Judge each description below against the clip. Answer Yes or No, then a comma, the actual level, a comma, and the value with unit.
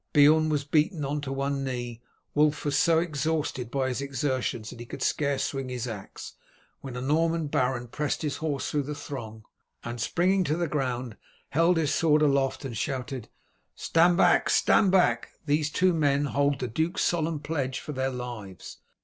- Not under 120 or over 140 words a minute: No, average, 180 wpm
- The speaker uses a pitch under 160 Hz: Yes, medium, 140 Hz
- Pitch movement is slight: No, average, 3.4 semitones